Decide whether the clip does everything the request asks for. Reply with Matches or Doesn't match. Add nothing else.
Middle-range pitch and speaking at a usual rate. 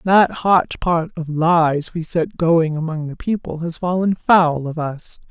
Matches